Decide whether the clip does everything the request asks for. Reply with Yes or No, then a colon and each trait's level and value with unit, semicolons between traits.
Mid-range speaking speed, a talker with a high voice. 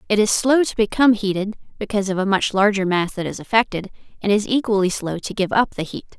No: fast, 235 wpm; high, 205 Hz